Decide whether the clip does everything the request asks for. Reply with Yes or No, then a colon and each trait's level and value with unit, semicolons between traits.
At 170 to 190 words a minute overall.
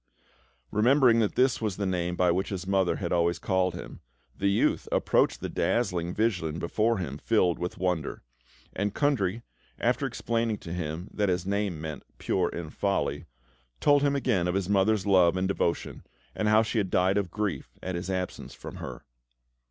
Yes: average, 180 wpm